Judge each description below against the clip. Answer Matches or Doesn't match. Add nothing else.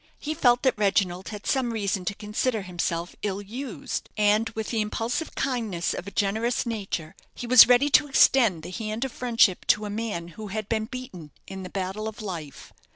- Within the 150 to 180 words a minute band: Doesn't match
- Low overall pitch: Doesn't match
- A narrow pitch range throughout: Doesn't match